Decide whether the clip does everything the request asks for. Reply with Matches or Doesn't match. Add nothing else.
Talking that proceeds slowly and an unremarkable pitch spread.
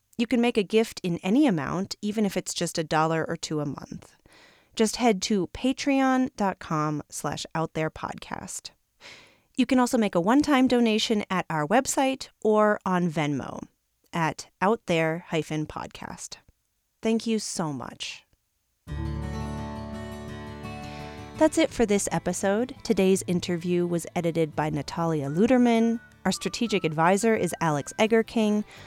Doesn't match